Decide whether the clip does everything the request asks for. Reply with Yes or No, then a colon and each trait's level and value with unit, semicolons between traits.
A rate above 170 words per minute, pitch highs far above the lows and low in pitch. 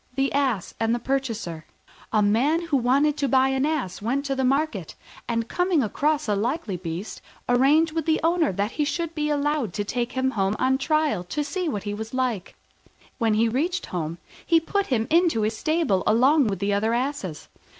No: average, 200 wpm; wide, 5.9 semitones; very high, 260 Hz